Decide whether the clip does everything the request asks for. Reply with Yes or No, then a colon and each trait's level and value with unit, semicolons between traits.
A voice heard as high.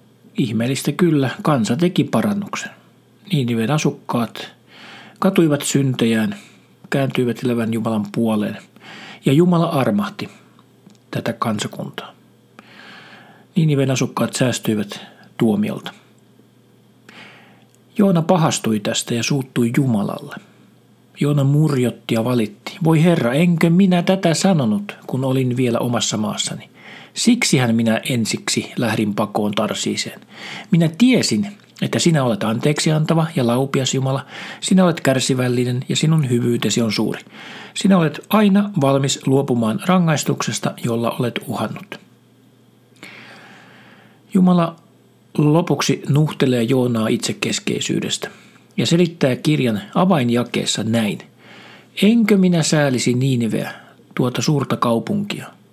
No: medium, 140 Hz